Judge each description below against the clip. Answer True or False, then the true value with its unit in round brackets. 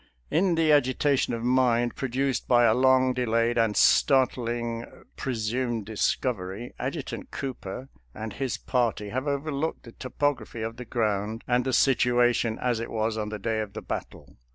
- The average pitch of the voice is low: True (120 Hz)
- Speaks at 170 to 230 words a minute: False (160 wpm)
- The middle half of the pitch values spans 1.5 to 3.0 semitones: True (2.6 semitones)